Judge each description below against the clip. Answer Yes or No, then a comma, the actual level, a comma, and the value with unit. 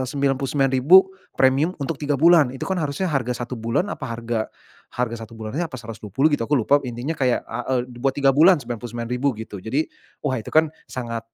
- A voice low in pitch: Yes, low, 130 Hz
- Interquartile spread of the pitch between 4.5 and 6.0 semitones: No, average, 3.7 semitones